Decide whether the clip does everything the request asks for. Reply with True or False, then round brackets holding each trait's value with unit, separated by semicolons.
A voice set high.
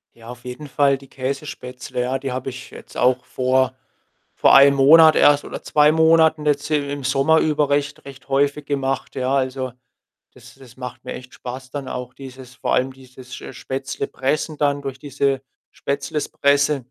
False (135 Hz)